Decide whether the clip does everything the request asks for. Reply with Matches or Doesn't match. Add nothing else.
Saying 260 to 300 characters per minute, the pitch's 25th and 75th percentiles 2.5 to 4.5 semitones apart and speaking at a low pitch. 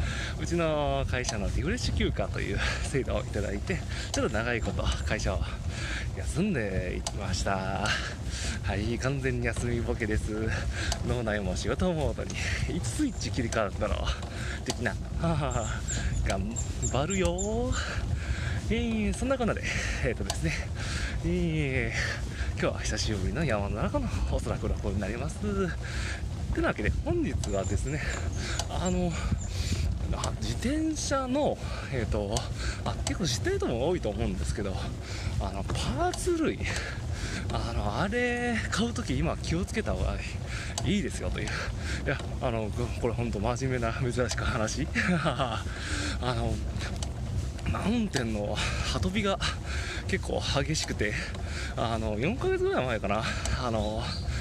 Matches